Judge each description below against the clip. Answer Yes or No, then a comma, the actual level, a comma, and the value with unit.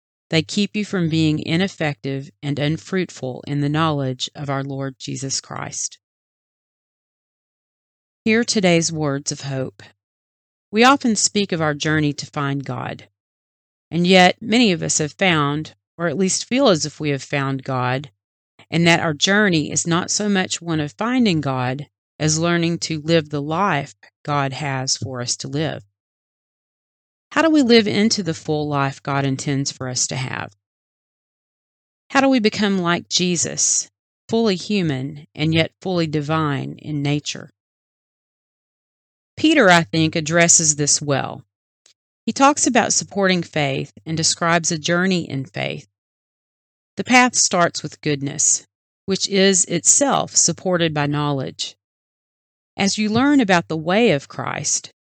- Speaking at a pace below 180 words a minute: Yes, average, 145 wpm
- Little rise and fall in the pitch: No, average, 5.1 semitones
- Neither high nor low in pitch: Yes, medium, 155 Hz